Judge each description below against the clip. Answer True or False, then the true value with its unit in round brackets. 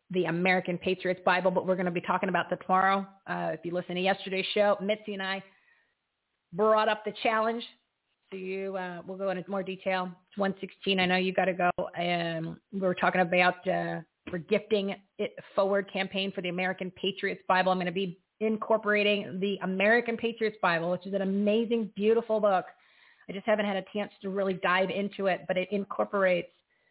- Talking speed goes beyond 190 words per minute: True (200 wpm)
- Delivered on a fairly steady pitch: True (1.9 semitones)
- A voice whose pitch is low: False (190 Hz)